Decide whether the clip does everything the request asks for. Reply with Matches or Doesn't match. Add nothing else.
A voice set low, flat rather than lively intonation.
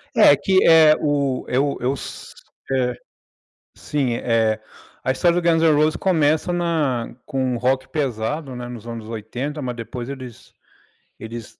Doesn't match